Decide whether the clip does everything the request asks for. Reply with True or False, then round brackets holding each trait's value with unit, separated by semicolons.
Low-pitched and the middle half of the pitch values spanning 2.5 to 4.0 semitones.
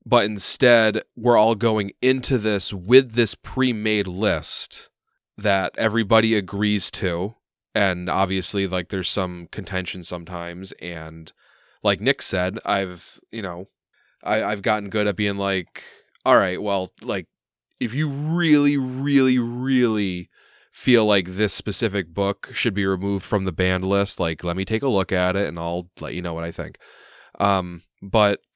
True (100 Hz; 3.5 semitones)